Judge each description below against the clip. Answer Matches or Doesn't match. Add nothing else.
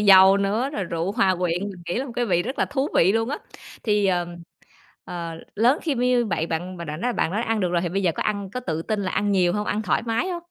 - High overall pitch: Matches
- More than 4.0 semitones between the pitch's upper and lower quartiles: Matches